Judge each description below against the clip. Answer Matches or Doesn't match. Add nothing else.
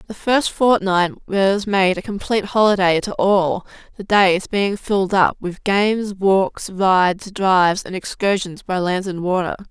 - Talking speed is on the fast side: Doesn't match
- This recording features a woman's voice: Matches